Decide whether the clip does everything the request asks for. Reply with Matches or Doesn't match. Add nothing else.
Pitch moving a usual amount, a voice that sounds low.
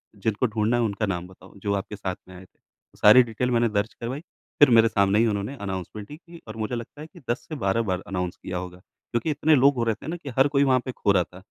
Matches